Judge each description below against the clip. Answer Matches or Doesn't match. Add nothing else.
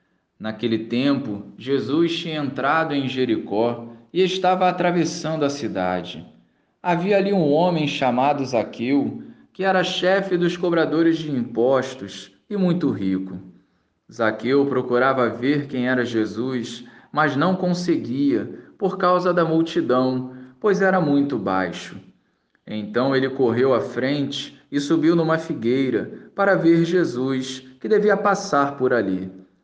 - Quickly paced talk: Doesn't match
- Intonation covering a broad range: Matches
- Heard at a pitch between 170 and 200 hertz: Doesn't match